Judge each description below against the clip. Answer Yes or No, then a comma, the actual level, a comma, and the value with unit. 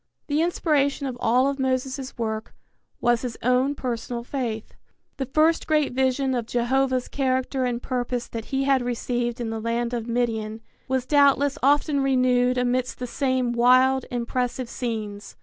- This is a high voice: Yes, very high, 255 Hz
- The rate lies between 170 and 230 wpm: No, average, 155 wpm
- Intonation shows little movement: Yes, narrow, 2.0 semitones